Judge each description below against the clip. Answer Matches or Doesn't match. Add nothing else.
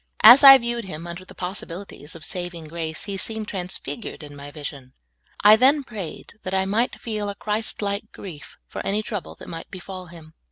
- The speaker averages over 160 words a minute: Matches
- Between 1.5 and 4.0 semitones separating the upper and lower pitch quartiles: Doesn't match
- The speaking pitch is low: Doesn't match